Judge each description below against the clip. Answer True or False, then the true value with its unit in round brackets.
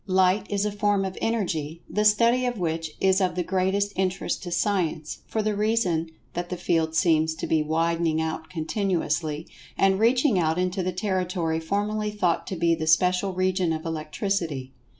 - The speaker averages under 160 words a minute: False (175 wpm)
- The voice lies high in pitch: False (180 Hz)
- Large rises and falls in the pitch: False (3.7 semitones)